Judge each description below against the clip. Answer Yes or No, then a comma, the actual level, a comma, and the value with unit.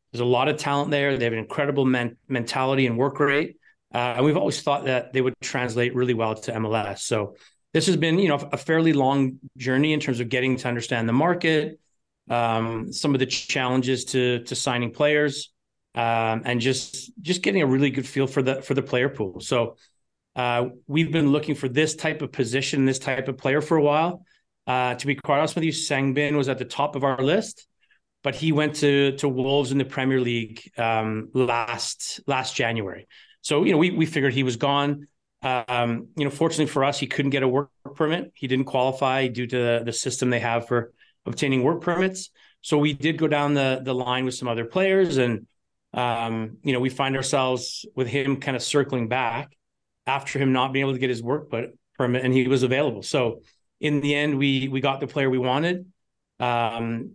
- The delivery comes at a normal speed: No, fast, 210 wpm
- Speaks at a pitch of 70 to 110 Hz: No, low, 135 Hz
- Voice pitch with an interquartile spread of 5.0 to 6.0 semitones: No, narrow, 2.6 semitones